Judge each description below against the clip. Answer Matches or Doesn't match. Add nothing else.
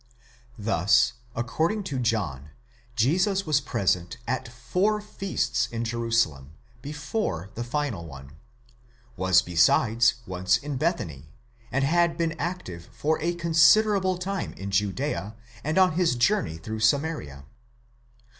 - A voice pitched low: Matches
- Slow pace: Matches